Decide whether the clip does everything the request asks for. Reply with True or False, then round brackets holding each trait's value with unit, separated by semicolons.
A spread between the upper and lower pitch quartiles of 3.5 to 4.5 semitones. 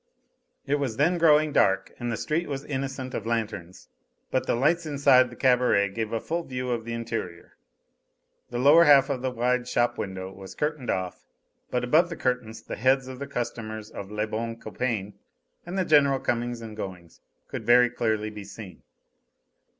True (3.9 semitones)